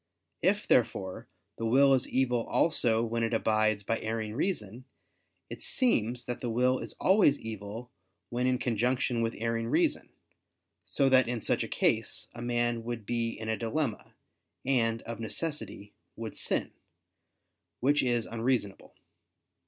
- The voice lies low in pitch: Yes, low, 120 Hz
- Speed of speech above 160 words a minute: No, average, 145 wpm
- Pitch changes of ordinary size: No, narrow, 2.2 semitones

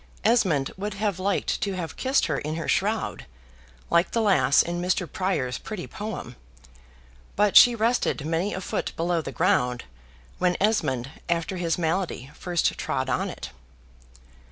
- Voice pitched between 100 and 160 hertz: No, medium, 180 Hz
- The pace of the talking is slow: No, average, 155 wpm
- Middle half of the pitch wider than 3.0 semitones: Yes, average, 4.1 semitones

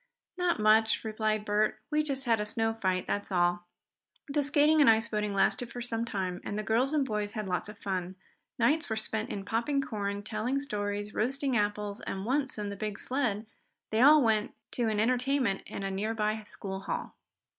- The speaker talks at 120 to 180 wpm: No, average, 195 wpm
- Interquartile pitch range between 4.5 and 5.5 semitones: No, average, 3.5 semitones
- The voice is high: Yes, high, 220 Hz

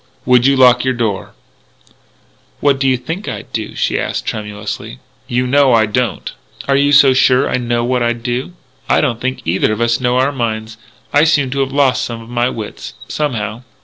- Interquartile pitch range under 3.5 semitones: Yes, average, 2.8 semitones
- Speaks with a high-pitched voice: No, low, 125 Hz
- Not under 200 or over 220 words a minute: Yes, fast, 205 wpm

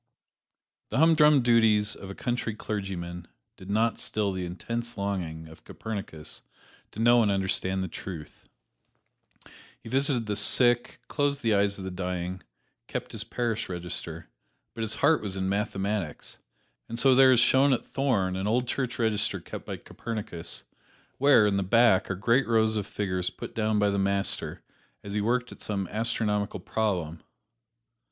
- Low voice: Yes, low, 105 Hz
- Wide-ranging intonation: No, average, 3.6 semitones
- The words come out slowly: No, average, 160 wpm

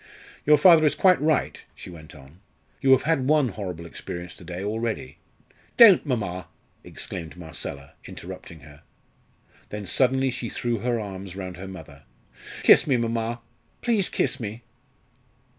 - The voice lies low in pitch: Yes, low, 105 Hz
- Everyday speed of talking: Yes, average, 150 wpm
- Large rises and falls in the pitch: Yes, wide, 6.9 semitones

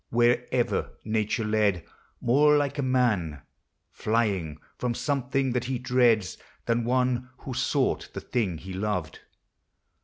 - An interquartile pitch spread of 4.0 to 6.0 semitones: No, average, 3.5 semitones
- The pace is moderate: No, slow, 125 wpm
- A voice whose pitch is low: Yes, low, 120 Hz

